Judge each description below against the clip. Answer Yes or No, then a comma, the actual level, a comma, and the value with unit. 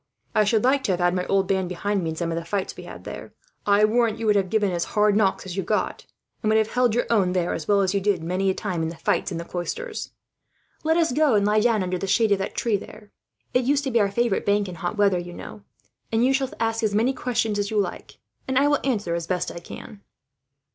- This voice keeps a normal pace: No, fast, 275 wpm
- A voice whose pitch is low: No, high, 205 Hz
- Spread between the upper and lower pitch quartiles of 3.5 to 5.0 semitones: Yes, average, 3.8 semitones